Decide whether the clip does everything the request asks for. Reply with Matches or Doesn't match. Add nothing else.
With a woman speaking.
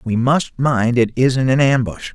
Doesn't match